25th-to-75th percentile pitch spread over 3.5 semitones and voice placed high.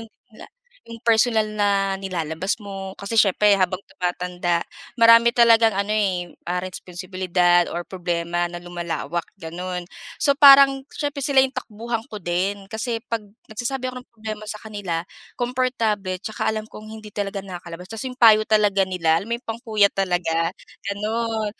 Yes: average, 3.9 semitones; high, 205 Hz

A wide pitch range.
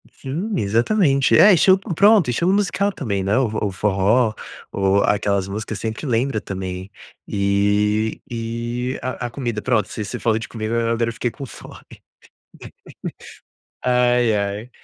No: average, 4.0 semitones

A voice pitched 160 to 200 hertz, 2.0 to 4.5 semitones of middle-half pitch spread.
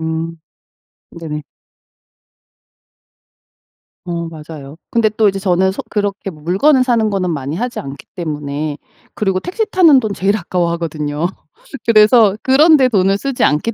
No: high, 190 Hz; wide, 5.5 semitones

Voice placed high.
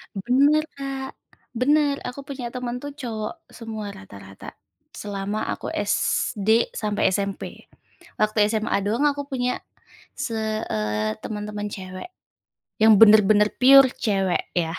Yes: high, 215 Hz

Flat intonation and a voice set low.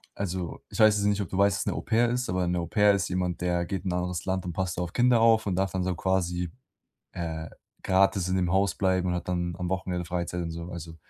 Yes: narrow, 1.9 semitones; very low, 90 Hz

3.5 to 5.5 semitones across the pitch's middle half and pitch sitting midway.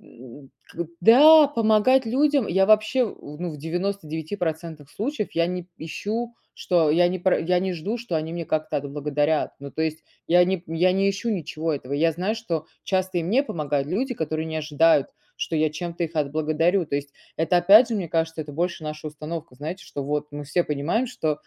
Yes: average, 4.2 semitones; medium, 170 Hz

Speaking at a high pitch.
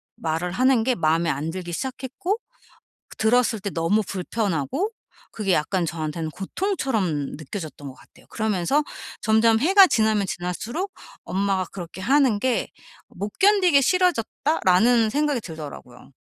Yes: high, 215 Hz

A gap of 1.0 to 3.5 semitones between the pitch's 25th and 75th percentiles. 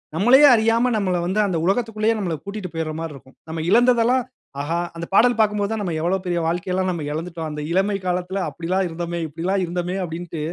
No: average, 4.0 semitones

